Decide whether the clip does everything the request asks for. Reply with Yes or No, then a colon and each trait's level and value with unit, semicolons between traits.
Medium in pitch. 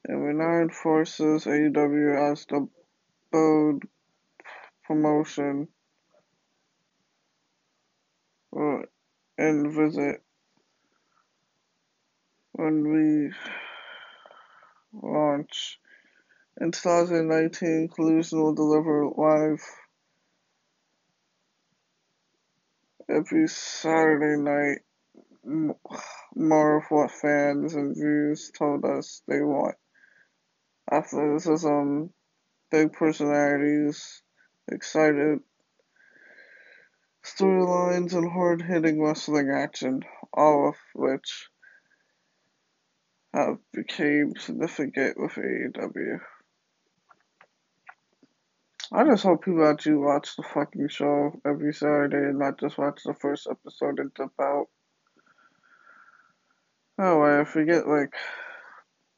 Yes: medium, 155 Hz